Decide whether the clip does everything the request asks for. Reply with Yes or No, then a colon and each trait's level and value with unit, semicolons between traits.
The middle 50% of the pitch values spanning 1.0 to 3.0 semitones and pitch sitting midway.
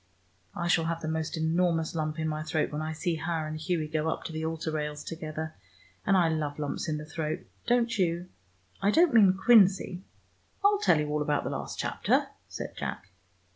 Yes: narrow, 2.4 semitones; medium, 160 Hz